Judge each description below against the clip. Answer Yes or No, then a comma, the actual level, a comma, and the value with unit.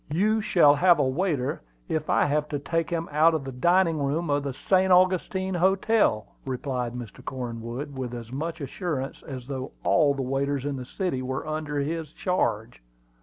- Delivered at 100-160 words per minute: No, average, 180 wpm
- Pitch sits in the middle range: Yes, medium, 145 Hz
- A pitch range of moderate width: Yes, average, 4.4 semitones